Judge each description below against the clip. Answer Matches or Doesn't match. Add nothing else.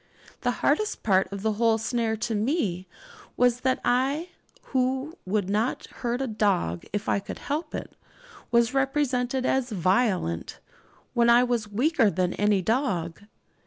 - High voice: Matches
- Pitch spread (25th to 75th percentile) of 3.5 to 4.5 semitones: Matches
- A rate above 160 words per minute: Doesn't match